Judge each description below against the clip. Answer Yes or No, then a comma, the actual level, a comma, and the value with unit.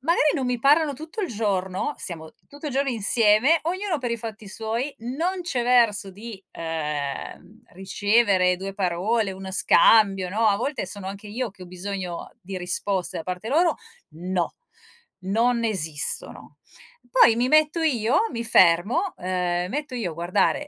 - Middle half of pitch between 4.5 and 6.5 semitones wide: Yes, wide, 5.6 semitones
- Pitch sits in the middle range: No, high, 215 Hz